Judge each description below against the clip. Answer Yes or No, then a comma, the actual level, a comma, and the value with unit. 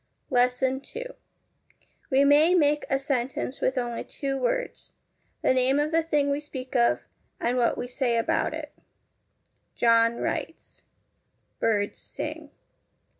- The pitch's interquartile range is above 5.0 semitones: No, average, 2.9 semitones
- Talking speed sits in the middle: No, slow, 130 wpm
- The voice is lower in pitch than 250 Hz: No, very high, 265 Hz